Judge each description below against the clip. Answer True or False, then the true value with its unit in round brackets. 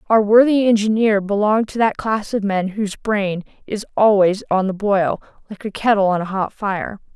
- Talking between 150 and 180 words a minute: False (195 wpm)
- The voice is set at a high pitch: True (205 Hz)